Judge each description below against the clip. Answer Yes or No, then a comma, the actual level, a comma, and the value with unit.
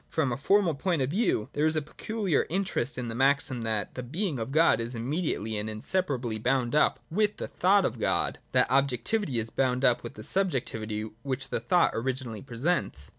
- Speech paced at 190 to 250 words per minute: Yes, average, 200 wpm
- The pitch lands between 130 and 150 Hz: Yes, low, 135 Hz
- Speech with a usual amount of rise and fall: No, wide, 6.2 semitones